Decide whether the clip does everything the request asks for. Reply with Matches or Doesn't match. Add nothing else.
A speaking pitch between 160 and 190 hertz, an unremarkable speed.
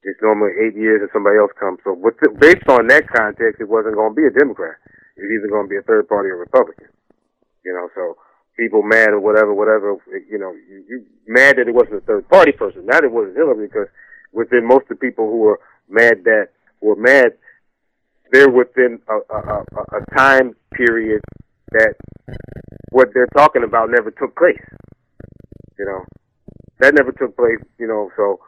Doesn't match